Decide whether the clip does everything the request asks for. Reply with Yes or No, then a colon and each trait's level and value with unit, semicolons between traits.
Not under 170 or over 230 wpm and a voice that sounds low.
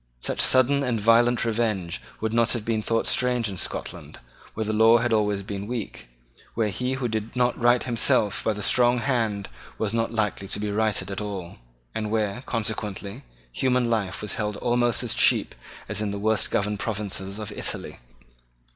Yes: average, 180 wpm; low, 110 Hz